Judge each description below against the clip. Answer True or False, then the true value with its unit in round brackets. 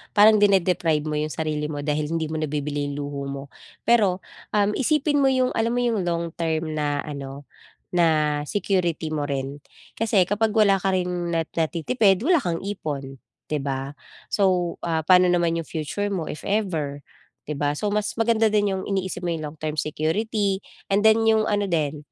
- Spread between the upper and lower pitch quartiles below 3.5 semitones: False (5.3 semitones)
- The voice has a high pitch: False (170 Hz)